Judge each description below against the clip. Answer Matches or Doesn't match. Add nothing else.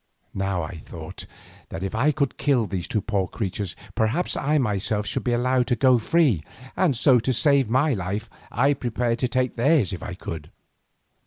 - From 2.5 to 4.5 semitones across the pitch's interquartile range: Doesn't match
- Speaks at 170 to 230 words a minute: Matches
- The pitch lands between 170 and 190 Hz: Doesn't match